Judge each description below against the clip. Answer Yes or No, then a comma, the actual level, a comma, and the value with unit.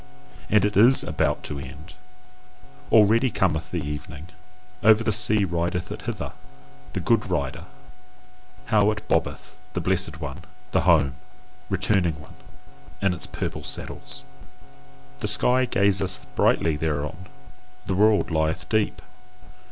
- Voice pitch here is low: Yes, very low, 90 Hz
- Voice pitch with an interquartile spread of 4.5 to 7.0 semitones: Yes, average, 4.8 semitones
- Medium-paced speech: No, slow, 130 wpm